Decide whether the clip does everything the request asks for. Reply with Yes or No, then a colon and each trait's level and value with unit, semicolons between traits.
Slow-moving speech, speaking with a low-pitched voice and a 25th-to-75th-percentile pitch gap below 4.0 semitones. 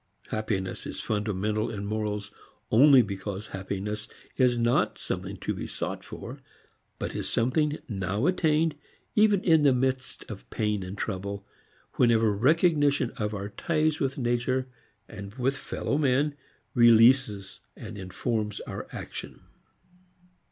No: slow, 130 wpm; low, 115 Hz; average, 4.9 semitones